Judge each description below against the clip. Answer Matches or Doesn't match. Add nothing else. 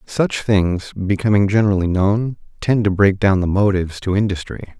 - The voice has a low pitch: Matches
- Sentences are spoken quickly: Doesn't match